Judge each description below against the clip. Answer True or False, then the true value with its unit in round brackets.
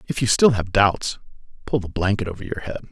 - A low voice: True (105 Hz)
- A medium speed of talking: False (225 wpm)